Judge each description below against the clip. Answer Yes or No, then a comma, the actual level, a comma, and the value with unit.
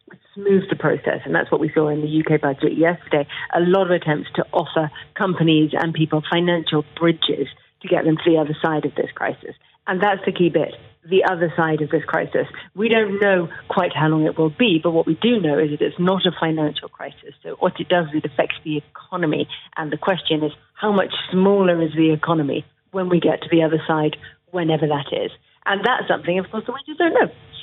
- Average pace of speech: No, fast, 230 wpm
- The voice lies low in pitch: No, medium, 165 Hz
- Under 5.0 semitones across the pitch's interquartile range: Yes, average, 2.9 semitones